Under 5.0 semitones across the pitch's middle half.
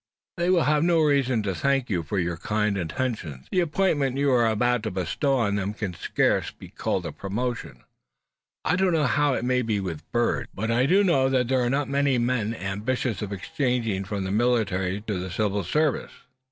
No: wide, 5.6 semitones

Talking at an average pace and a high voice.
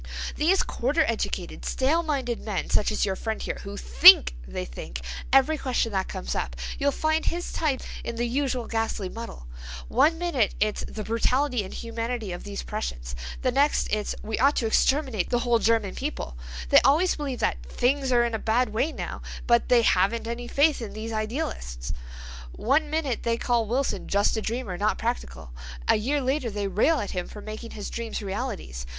Yes: average, 185 wpm; high, 230 Hz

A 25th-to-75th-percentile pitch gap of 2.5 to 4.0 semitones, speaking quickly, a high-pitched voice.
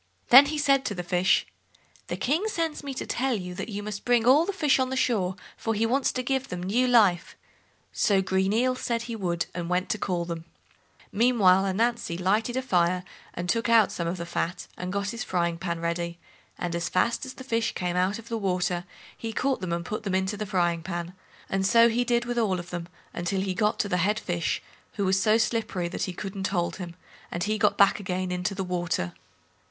No: average, 4.6 semitones; fast, 225 wpm; high, 195 Hz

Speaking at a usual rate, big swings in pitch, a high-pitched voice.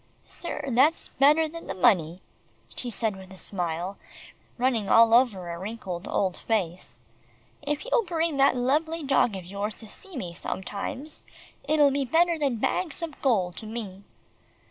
Yes: average, 160 wpm; wide, 7.5 semitones; high, 235 Hz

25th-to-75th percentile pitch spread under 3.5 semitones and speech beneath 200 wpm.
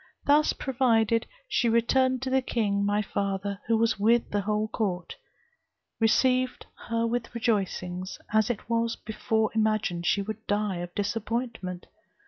Yes: narrow, 2.6 semitones; slow, 135 wpm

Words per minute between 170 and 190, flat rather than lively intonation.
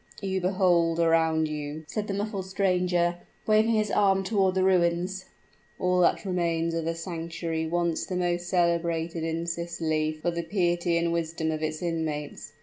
No: average, 160 wpm; narrow, 2.1 semitones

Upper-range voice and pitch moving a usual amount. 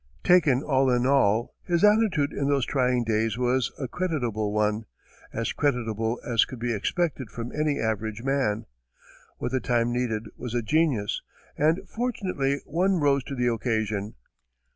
No: low, 125 Hz; average, 4.2 semitones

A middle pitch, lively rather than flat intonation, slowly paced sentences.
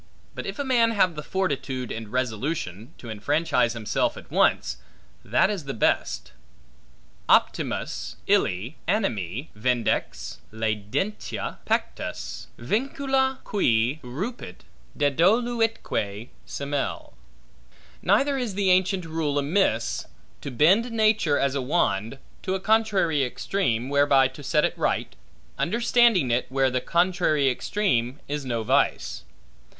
Yes: medium, 145 Hz; wide, 8.6 semitones; slow, 120 wpm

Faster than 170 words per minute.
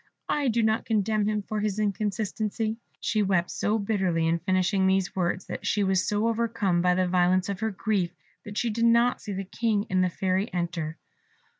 Yes: average, 195 wpm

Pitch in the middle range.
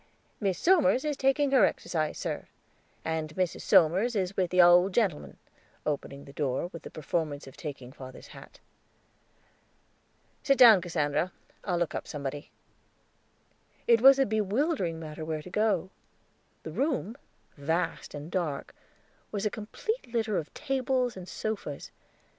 Yes: medium, 180 Hz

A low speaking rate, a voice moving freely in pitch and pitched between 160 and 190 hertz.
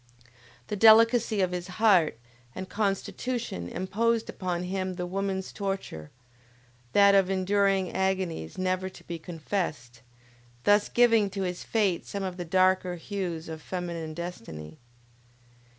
No: slow, 130 wpm; narrow, 2.4 semitones; medium, 185 Hz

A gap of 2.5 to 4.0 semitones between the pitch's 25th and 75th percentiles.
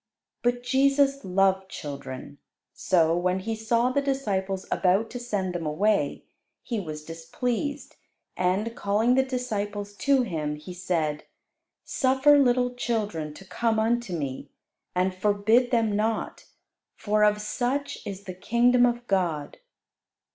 No: average, 5.1 semitones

